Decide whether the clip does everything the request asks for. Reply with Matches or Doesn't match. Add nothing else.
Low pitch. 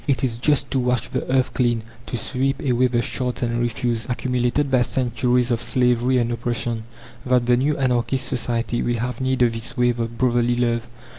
Matches